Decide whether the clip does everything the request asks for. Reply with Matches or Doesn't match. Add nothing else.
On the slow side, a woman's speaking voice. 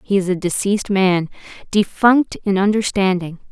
Matches